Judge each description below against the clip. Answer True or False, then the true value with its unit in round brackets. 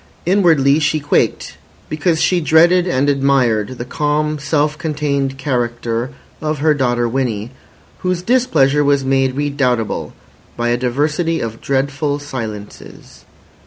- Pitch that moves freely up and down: False (3.4 semitones)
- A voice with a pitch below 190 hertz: True (140 Hz)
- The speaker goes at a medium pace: False (125 wpm)